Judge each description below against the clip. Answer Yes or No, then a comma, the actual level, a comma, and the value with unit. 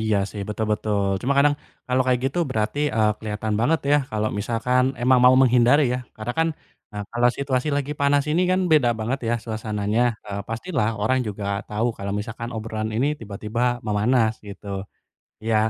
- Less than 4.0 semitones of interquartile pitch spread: Yes, average, 3.3 semitones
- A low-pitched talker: Yes, low, 115 Hz